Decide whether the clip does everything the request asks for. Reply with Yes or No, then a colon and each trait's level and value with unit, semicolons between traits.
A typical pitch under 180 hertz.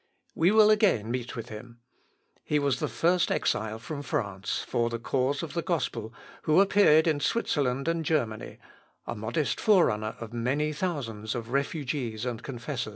Yes: low, 135 Hz